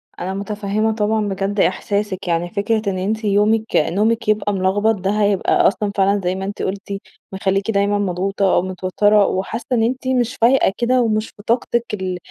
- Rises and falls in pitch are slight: Yes, narrow, 2.3 semitones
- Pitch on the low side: No, high, 205 Hz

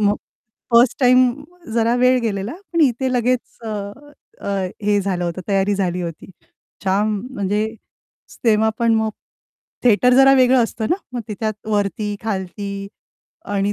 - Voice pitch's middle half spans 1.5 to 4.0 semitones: Yes, average, 3.6 semitones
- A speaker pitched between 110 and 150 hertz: No, high, 215 Hz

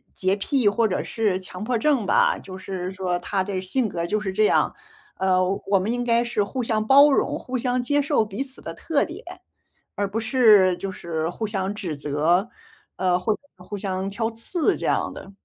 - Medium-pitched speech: No, high, 205 Hz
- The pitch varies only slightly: No, average, 4.2 semitones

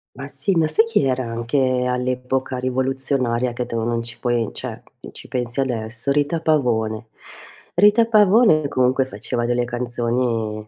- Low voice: Yes, low, 125 Hz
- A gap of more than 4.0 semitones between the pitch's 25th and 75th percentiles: No, average, 2.8 semitones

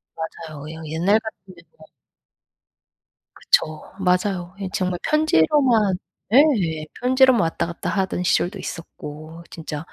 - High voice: No, medium, 180 Hz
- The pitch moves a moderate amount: Yes, average, 4.7 semitones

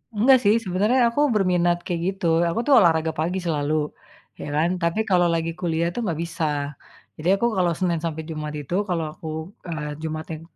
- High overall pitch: No, medium, 170 Hz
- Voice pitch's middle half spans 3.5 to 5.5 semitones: No, narrow, 2.6 semitones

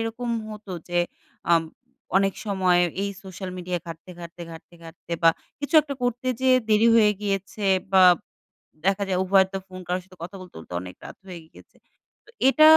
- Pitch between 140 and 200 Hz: Yes, high, 190 Hz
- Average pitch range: Yes, average, 3.1 semitones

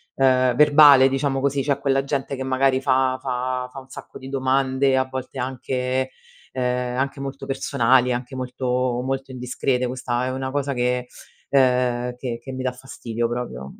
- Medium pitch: No, low, 130 Hz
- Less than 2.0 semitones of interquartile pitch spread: Yes, narrow, 1.3 semitones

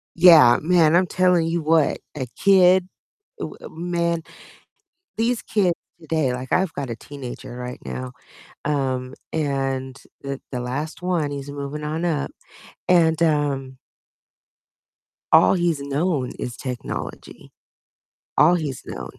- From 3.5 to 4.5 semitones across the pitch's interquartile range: Yes, average, 4.2 semitones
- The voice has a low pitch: No, medium, 150 Hz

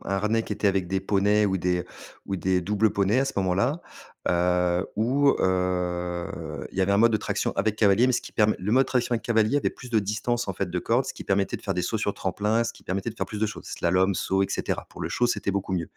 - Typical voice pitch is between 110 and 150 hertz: No, low, 100 Hz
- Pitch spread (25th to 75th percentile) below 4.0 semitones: Yes, average, 3.2 semitones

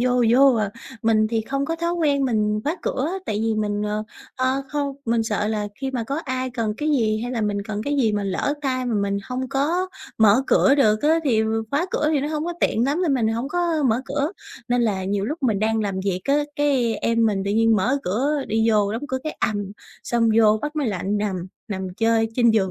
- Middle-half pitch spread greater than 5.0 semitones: No, average, 4.6 semitones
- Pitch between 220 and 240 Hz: Yes, high, 230 Hz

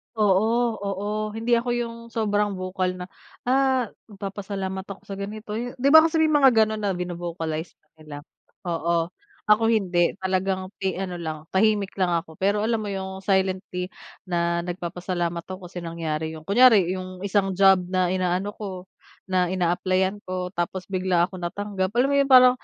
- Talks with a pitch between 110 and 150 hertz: No, high, 190 Hz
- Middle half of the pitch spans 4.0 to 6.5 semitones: No, average, 2.8 semitones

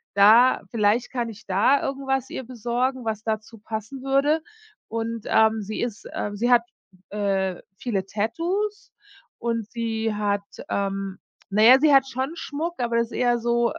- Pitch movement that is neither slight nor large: Yes, average, 3.6 semitones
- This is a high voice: Yes, high, 230 Hz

